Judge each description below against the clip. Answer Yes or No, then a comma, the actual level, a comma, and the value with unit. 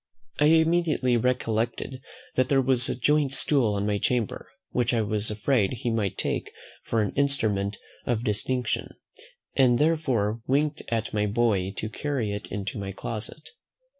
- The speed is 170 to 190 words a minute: No, average, 155 wpm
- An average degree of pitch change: Yes, average, 4.2 semitones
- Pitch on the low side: Yes, low, 120 Hz